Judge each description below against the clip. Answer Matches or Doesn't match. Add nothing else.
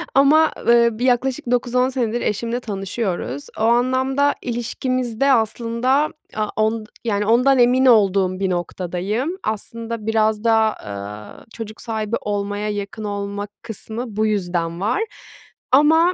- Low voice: Doesn't match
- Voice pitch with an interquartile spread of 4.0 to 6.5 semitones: Doesn't match